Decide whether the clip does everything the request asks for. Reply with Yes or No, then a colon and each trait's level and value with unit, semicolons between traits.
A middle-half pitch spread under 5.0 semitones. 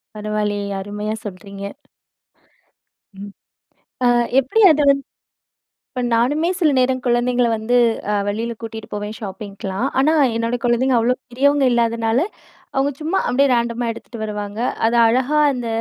Yes: average, 3.5 semitones